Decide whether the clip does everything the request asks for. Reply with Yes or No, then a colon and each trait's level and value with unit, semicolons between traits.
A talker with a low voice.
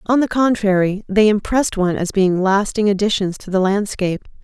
No: high, 200 Hz